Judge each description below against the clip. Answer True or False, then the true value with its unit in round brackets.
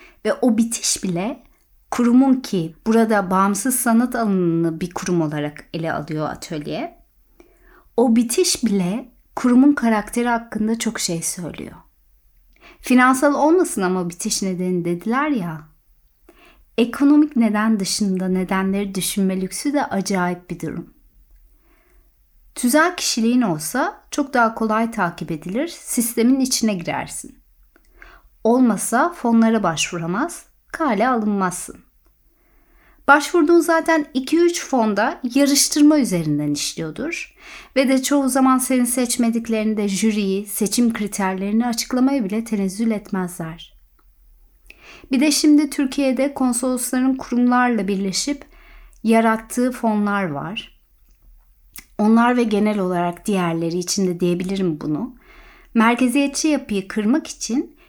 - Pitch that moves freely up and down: True (5.9 semitones)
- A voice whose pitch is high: True (230 Hz)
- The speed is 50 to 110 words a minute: True (105 wpm)